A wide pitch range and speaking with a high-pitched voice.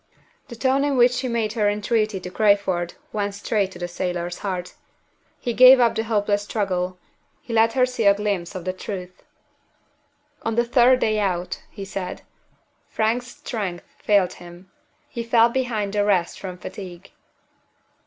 No: average, 4.1 semitones; high, 205 Hz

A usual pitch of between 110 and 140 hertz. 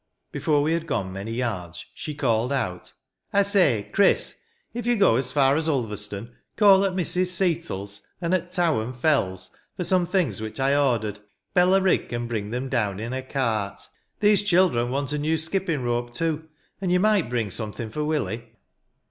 Yes: low, 135 Hz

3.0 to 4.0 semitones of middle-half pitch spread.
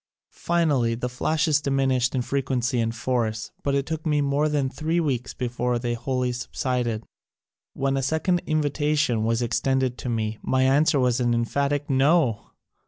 Yes: average, 3.3 semitones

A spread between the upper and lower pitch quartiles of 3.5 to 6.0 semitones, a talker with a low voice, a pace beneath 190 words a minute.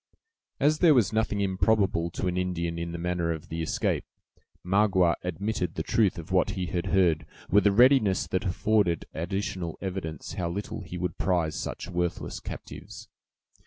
No: average, 3.0 semitones; very low, 90 Hz; average, 165 wpm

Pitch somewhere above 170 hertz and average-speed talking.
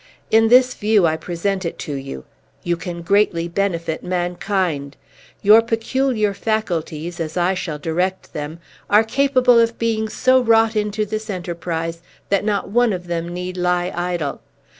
Yes: medium, 185 Hz; average, 155 wpm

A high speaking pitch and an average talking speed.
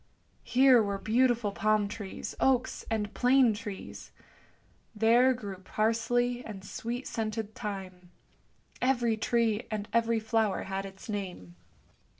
No: high, 220 Hz; slow, 120 wpm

